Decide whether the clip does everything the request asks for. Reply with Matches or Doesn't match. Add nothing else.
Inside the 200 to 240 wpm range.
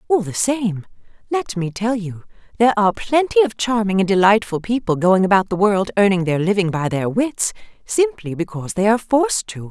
Doesn't match